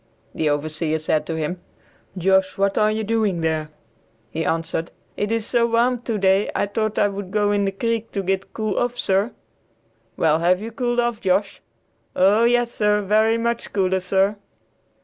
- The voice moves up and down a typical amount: Yes, average, 3.5 semitones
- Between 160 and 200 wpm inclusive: Yes, average, 180 wpm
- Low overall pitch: No, high, 200 Hz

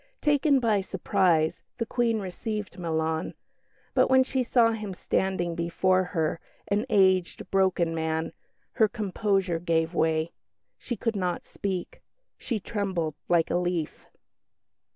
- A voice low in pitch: No, medium, 185 Hz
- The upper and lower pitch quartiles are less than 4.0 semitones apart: No, average, 4.3 semitones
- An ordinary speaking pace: No, slow, 130 wpm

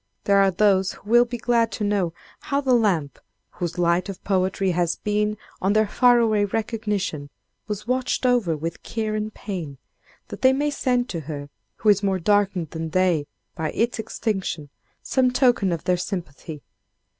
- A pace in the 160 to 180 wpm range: Yes, average, 175 wpm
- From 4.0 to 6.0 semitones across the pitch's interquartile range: Yes, average, 4.6 semitones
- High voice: Yes, high, 200 Hz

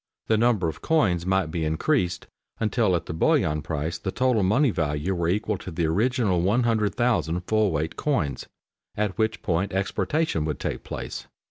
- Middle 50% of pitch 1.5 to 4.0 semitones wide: No, average, 5.1 semitones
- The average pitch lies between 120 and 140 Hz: No, very low, 95 Hz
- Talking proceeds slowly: No, average, 165 wpm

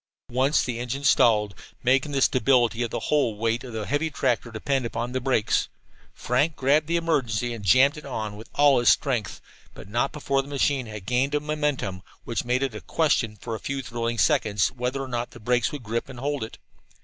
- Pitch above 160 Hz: No, low, 125 Hz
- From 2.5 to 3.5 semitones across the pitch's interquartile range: Yes, average, 3.2 semitones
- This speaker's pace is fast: Yes, fast, 210 wpm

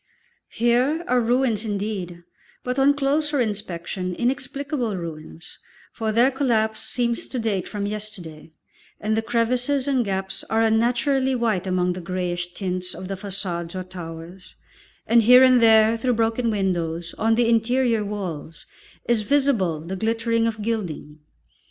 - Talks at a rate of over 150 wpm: No, average, 145 wpm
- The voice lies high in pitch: Yes, high, 220 Hz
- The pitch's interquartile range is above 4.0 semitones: Yes, average, 4.8 semitones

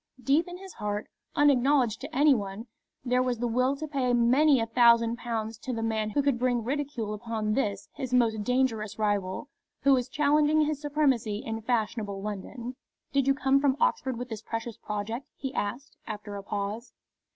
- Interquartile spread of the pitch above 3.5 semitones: Yes, average, 4.0 semitones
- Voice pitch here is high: Yes, high, 240 Hz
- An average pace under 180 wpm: No, average, 185 wpm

